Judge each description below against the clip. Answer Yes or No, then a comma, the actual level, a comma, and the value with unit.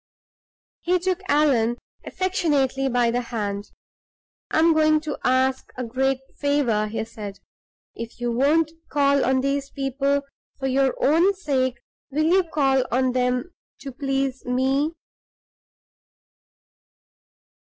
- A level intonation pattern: No, average, 3.1 semitones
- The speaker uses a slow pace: Yes, slow, 120 wpm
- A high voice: Yes, very high, 270 Hz